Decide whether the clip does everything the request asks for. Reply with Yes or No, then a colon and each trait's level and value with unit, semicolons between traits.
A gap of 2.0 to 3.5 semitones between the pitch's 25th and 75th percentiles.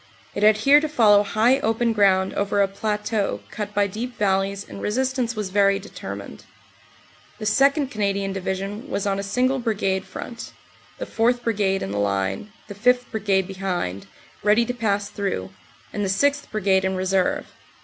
Yes: average, 3.0 semitones